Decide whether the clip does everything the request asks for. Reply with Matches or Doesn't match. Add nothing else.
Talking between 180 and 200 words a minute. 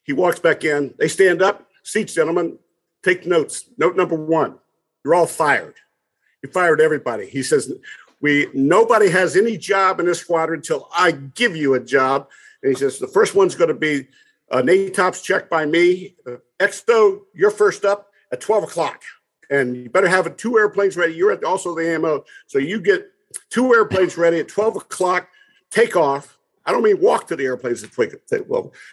Matches